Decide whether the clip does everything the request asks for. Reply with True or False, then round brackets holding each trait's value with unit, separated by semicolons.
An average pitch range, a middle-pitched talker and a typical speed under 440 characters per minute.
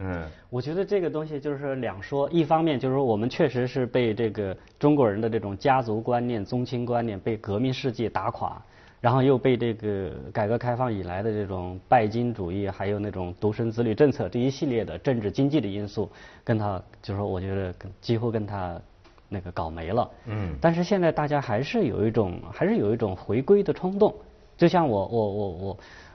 False (4.6 semitones; 115 Hz; 305 characters per minute)